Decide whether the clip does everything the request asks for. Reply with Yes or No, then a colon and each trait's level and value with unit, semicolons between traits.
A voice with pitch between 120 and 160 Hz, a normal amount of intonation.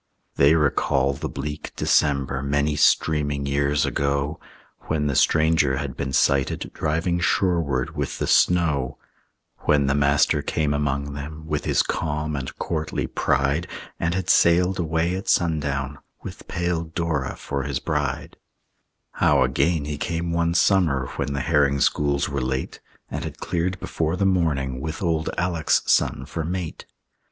No: very low, 75 Hz; average, 3.0 semitones